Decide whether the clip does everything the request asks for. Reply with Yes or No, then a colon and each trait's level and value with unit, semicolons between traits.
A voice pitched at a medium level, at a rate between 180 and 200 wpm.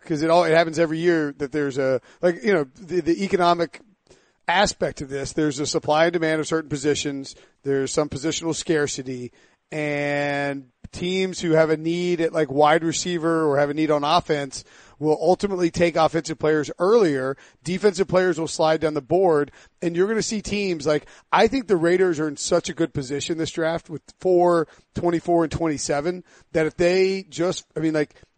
Yes: medium, 160 Hz; average, 190 wpm